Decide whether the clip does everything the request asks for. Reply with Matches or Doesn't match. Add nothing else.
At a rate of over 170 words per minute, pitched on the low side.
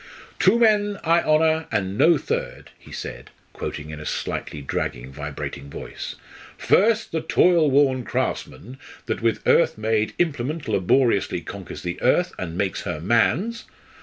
Doesn't match